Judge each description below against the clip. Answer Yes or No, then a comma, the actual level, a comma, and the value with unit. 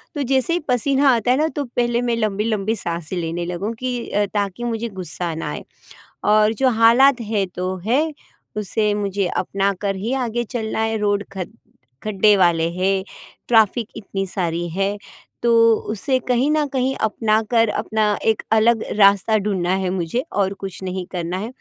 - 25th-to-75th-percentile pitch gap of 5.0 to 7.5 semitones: No, average, 3.7 semitones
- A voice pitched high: Yes, high, 210 Hz